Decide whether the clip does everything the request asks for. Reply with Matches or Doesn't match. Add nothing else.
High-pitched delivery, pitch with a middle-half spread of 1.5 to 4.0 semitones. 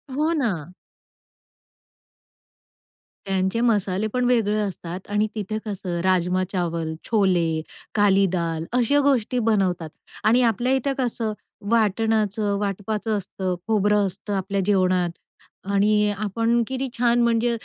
Matches